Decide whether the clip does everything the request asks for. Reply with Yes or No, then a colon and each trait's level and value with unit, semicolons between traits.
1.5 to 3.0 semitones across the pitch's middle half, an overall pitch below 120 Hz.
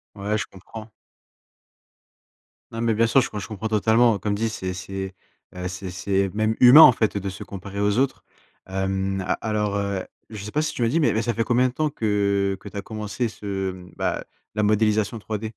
Yes: narrow, 2.6 semitones; low, 105 Hz